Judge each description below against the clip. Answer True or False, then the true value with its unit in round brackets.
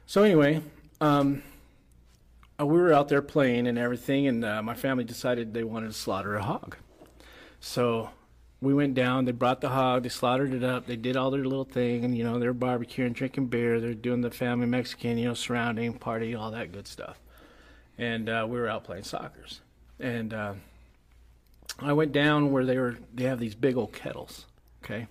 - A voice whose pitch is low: True (125 Hz)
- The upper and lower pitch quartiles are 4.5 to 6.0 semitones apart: False (2.4 semitones)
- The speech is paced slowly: False (195 wpm)